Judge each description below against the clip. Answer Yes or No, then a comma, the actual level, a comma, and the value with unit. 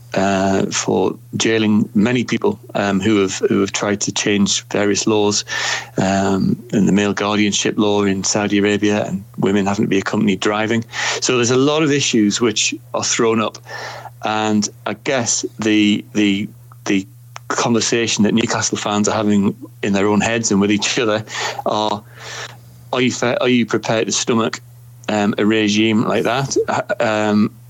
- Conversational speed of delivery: Yes, average, 165 wpm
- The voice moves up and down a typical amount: No, narrow, 2.3 semitones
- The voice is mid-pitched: No, low, 105 Hz